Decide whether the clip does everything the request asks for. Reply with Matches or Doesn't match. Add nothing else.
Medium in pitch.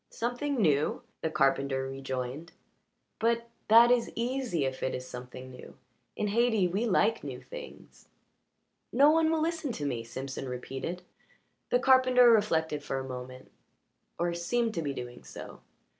Matches